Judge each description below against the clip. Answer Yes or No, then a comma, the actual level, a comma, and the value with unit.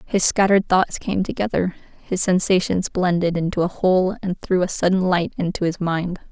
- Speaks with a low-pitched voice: No, medium, 180 Hz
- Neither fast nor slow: Yes, average, 180 wpm